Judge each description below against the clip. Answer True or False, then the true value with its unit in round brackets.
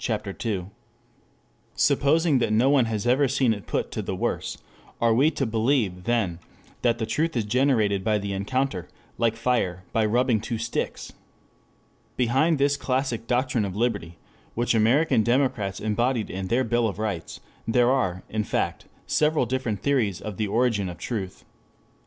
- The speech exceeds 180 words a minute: False (160 wpm)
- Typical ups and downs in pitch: True (3.6 semitones)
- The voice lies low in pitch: True (115 Hz)